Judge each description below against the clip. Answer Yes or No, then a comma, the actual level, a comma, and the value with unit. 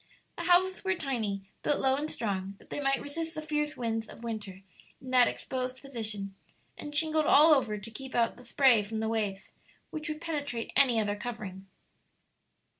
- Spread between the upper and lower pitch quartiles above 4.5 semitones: Yes, wide, 5.5 semitones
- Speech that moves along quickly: No, average, 185 wpm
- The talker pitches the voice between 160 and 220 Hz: No, very high, 250 Hz